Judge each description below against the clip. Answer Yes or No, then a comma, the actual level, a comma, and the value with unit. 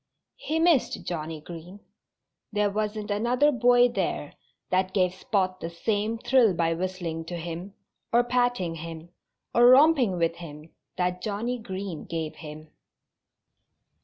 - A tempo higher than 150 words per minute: No, slow, 135 wpm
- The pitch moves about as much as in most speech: No, wide, 5.9 semitones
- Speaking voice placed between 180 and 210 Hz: Yes, high, 190 Hz